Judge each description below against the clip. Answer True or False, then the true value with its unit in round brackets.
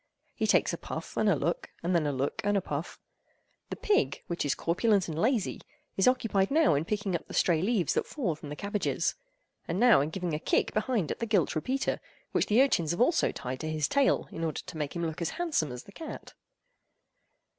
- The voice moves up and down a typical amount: False (6.6 semitones)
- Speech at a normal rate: False (220 wpm)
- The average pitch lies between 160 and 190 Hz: True (185 Hz)